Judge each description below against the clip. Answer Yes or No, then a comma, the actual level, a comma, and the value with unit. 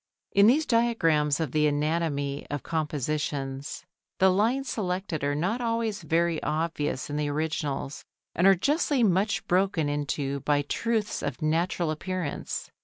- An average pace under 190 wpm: Yes, average, 140 wpm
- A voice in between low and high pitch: Yes, medium, 160 Hz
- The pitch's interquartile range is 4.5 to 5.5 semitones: Yes, average, 5.1 semitones